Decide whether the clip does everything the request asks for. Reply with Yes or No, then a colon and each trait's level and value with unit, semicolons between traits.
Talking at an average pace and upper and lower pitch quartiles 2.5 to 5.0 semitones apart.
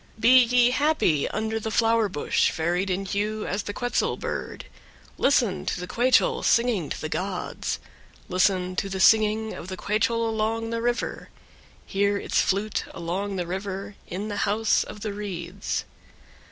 Yes: average, 165 wpm; average, 3.2 semitones